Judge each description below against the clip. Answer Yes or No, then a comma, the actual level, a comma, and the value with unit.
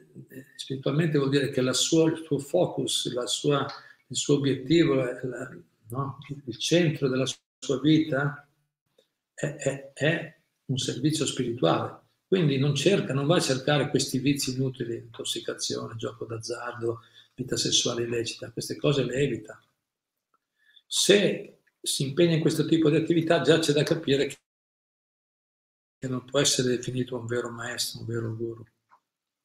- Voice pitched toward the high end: No, low, 135 Hz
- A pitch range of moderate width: Yes, average, 3.6 semitones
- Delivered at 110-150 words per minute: Yes, average, 145 wpm